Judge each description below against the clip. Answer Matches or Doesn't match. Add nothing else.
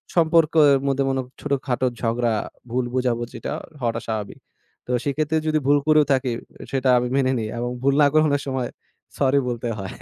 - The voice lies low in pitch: Matches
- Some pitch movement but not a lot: Matches